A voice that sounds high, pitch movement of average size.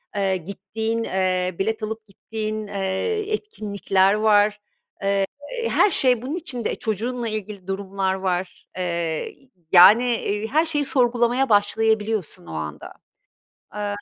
Yes: high, 210 Hz; average, 3.2 semitones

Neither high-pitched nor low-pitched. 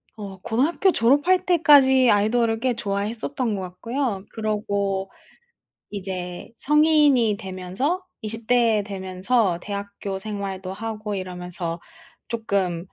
No: high, 210 Hz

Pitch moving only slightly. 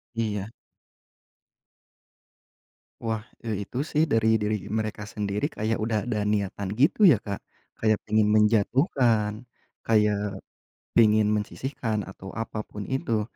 Yes: narrow, 1.5 semitones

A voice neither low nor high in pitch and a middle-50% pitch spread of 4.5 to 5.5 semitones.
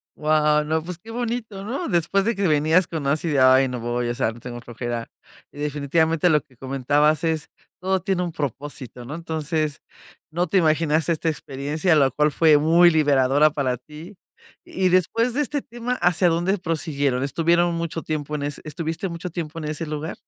No: medium, 155 Hz; average, 3.2 semitones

